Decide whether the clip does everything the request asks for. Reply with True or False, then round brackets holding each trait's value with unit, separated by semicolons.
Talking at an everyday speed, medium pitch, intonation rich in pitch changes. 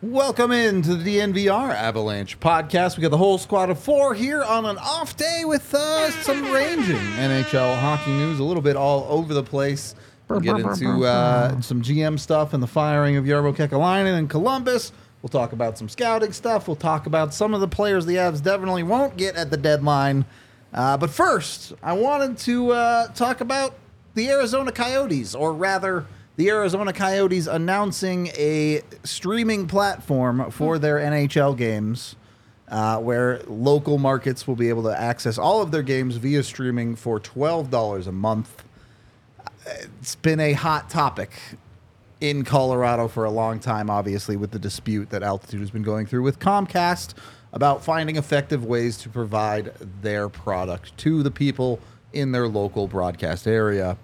True (170 wpm; 145 Hz; 8.5 semitones)